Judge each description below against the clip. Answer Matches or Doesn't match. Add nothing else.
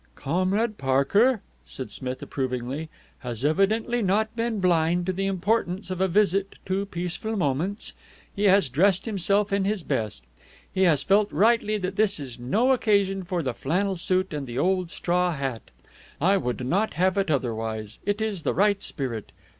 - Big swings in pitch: Matches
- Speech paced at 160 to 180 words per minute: Matches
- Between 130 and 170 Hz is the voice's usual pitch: Doesn't match